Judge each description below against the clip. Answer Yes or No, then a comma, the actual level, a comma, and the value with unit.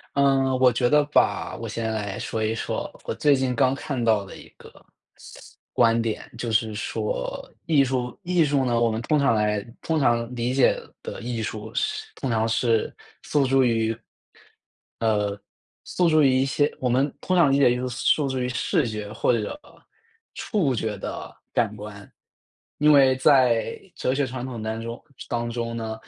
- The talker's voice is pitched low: Yes, low, 120 Hz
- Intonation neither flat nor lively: Yes, average, 3.3 semitones